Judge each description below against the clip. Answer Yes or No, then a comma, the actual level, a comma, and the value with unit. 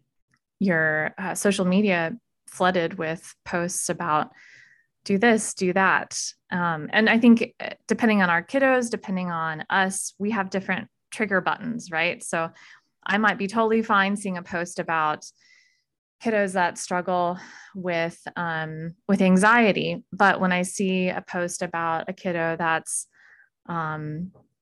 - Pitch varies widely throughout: No, average, 3.5 semitones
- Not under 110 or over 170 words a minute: Yes, average, 140 wpm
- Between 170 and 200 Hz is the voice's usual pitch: Yes, medium, 185 Hz